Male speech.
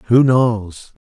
Yes: male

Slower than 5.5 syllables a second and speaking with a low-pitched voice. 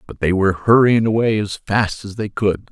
Yes: 5.1 syllables/s; low, 105 Hz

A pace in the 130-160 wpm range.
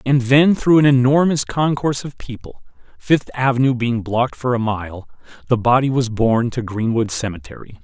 No: average, 170 wpm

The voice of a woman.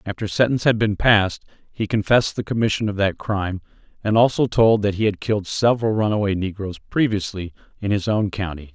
No: male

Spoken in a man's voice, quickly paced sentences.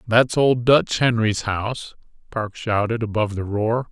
No: male; average, 155 wpm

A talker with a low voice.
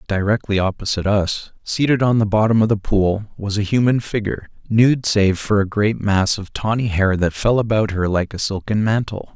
Yes: low, 105 Hz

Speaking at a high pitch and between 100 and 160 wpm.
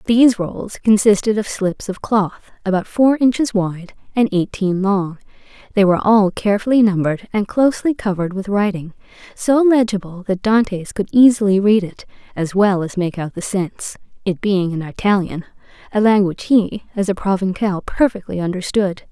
Yes: high, 200 Hz; average, 155 wpm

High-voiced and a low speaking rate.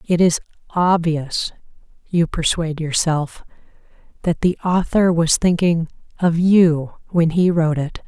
No: medium, 165 Hz; slow, 125 wpm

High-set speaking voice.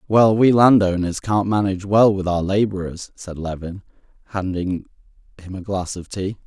No: very low, 95 Hz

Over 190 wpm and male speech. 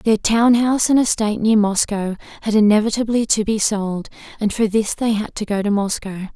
No: average, 200 wpm; female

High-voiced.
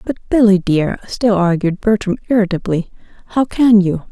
Yes: high, 200 Hz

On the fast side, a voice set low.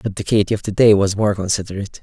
Yes: fast, 265 wpm; low, 100 Hz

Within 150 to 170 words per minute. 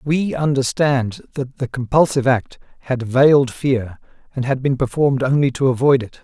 Yes: average, 165 wpm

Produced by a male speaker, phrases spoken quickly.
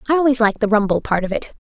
No: female; fast, 295 wpm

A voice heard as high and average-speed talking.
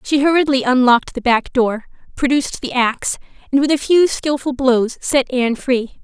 Yes: very high, 260 Hz; average, 180 wpm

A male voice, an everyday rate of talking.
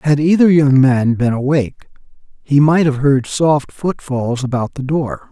Yes: male; average, 170 wpm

